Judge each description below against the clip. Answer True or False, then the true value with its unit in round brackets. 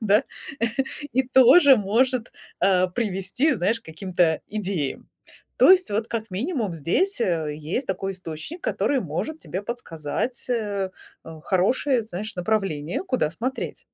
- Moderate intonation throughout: False (5.8 semitones)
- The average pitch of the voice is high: True (205 Hz)